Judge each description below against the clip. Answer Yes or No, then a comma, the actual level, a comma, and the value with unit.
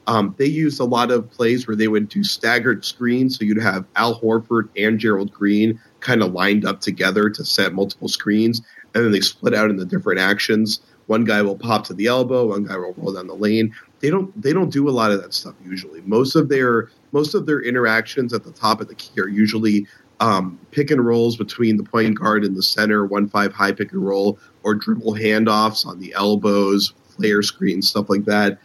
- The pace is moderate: No, fast, 220 wpm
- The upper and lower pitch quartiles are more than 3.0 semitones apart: No, narrow, 2.5 semitones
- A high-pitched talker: No, low, 110 Hz